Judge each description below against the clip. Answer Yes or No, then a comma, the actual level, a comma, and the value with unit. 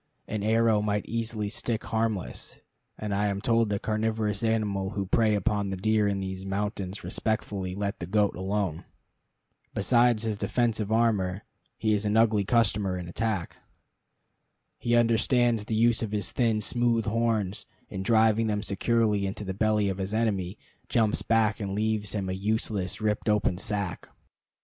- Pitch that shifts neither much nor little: No, narrow, 2.1 semitones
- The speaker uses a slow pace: No, average, 160 wpm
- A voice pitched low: Yes, low, 105 Hz